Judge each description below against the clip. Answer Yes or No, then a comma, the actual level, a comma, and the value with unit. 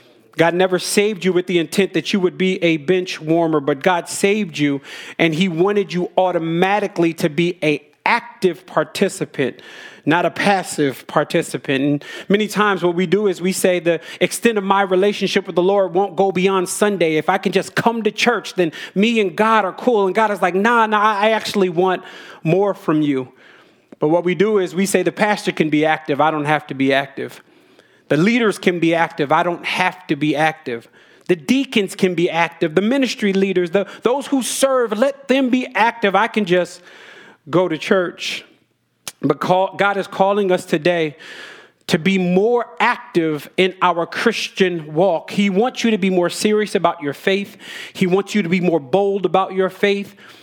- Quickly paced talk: No, average, 195 wpm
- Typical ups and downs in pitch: Yes, average, 3.2 semitones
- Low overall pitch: No, medium, 185 Hz